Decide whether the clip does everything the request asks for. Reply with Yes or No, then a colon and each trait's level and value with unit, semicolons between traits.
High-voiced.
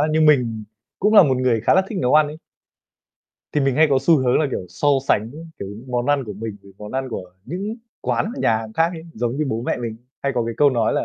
No: low, 130 Hz